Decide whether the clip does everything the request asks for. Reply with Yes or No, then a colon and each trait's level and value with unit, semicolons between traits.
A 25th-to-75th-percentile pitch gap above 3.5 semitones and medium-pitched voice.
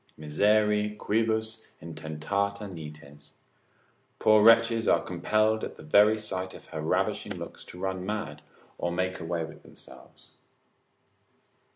No: average, 4.8 semitones; very low, 95 Hz